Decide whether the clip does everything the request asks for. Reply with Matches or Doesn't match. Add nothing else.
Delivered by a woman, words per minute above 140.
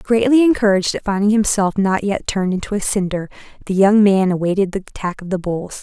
Matches